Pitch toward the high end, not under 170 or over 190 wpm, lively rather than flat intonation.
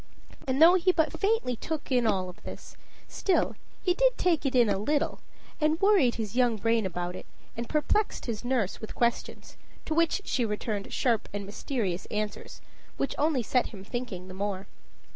Yes: high, 245 Hz; average, 180 wpm; wide, 7.1 semitones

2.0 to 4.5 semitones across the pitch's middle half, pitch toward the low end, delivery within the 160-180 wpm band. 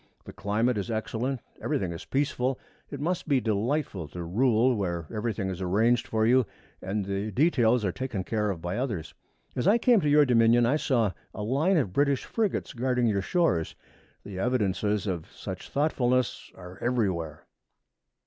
No: average, 5.1 semitones; low, 115 Hz; average, 170 wpm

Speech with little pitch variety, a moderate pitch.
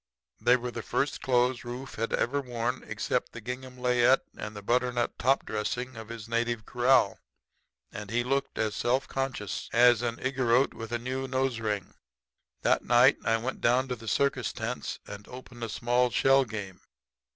No: narrow, 2.0 semitones; low, 120 Hz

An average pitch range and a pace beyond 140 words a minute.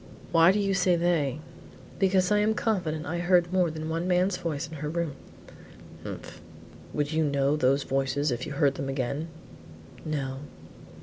Yes: average, 4.0 semitones; average, 170 wpm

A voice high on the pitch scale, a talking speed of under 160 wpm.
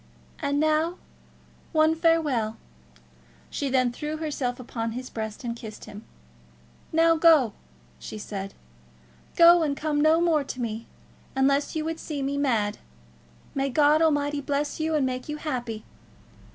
Yes: very high, 285 Hz; average, 145 wpm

